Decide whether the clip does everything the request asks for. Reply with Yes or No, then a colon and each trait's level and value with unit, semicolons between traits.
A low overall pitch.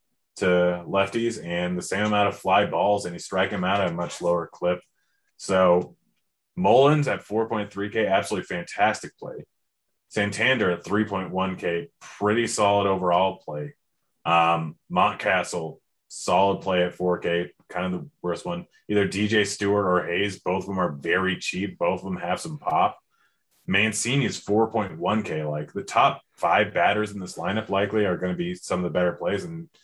Yes: very low, 95 Hz